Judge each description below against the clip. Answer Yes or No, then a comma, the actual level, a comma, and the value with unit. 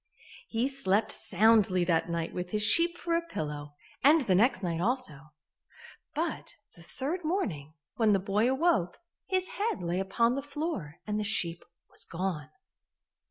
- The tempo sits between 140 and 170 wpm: Yes, average, 160 wpm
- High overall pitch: Yes, high, 210 Hz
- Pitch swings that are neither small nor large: No, wide, 8.0 semitones